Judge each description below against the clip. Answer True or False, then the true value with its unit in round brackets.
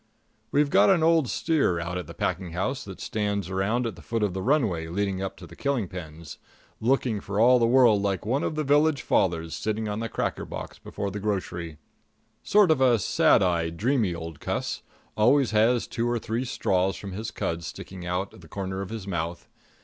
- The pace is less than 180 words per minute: False (205 wpm)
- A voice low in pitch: True (105 Hz)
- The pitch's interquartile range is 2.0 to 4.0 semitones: False (5.2 semitones)